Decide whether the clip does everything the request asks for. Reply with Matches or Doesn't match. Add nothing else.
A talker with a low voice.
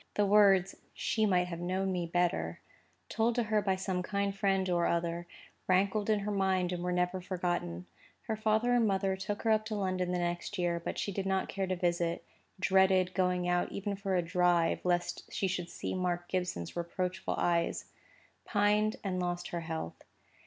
Doesn't match